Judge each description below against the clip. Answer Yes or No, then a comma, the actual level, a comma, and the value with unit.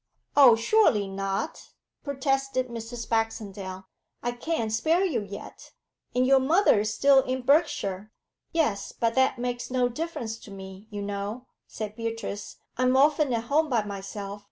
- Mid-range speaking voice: No, high, 235 Hz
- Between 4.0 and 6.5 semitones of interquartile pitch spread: Yes, average, 4.8 semitones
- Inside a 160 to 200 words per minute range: No, average, 150 wpm